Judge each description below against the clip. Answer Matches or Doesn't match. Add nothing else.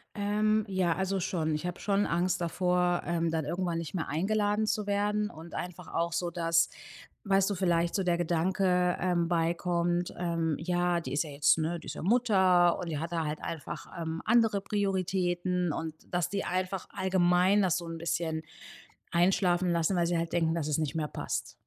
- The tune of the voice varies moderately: Doesn't match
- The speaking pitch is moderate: Matches